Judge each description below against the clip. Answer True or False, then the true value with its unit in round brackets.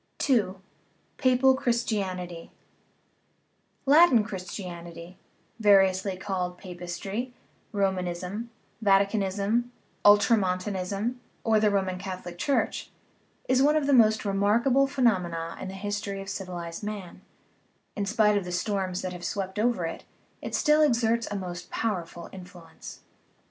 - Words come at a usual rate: False (125 wpm)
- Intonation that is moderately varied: True (3.6 semitones)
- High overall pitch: True (200 Hz)